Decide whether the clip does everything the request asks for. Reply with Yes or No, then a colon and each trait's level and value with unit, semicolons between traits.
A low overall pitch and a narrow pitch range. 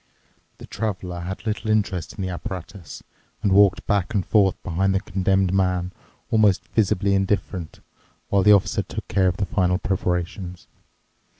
Yes: very low, 95 Hz; narrow, 1.8 semitones